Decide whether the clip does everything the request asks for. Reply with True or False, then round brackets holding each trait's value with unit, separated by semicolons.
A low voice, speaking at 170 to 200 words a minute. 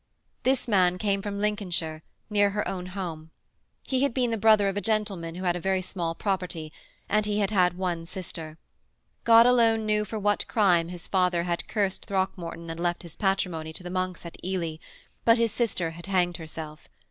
False (185 Hz; 195 wpm)